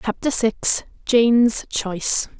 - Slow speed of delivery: Yes, slow, 100 wpm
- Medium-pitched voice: No, high, 225 Hz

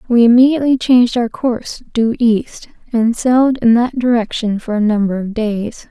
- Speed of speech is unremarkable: Yes, average, 175 wpm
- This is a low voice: No, high, 235 Hz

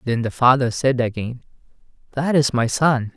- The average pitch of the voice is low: Yes, low, 125 Hz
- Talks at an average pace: Yes, average, 170 wpm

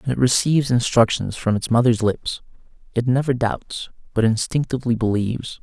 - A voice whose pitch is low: Yes, low, 120 Hz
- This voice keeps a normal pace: Yes, average, 150 wpm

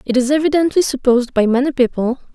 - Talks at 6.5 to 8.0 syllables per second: Yes, 6.6 syllables/s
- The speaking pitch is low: No, very high, 265 Hz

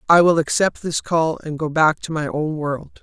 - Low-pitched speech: No, medium, 160 Hz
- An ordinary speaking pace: No, fast, 240 wpm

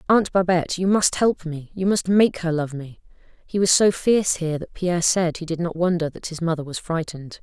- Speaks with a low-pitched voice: No, medium, 175 Hz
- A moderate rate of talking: No, fast, 225 wpm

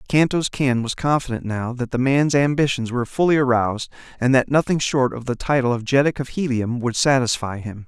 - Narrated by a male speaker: Yes, male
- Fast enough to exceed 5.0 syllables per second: Yes, 5.6 syllables/s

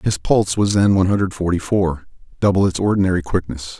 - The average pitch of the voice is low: Yes, very low, 95 Hz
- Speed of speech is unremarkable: Yes, average, 190 wpm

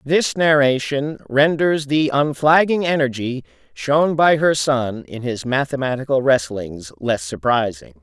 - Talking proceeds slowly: Yes, slow, 120 wpm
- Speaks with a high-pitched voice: No, medium, 140 Hz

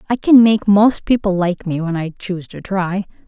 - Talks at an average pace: No, fast, 220 wpm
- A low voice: No, high, 195 Hz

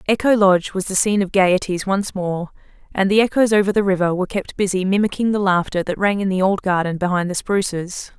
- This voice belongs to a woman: Yes, female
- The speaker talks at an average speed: No, fast, 220 wpm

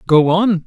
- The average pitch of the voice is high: No, medium, 180 Hz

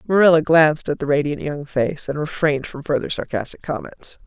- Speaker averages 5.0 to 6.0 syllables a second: Yes, 5.7 syllables/s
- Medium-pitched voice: Yes, medium, 155 Hz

